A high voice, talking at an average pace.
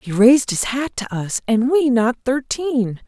Yes: high, 245 Hz; average, 195 wpm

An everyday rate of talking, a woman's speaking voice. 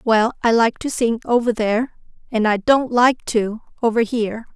Yes: average, 185 wpm; female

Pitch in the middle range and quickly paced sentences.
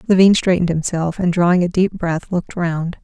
No: medium, 175 Hz; average, 195 wpm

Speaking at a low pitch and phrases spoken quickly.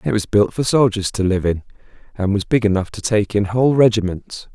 Yes: low, 105 Hz; fast, 225 wpm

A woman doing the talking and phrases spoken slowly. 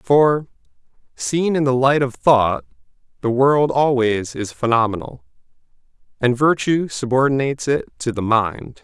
No: male; slow, 130 wpm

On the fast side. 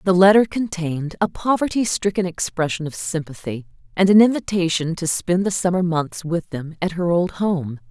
No: average, 175 wpm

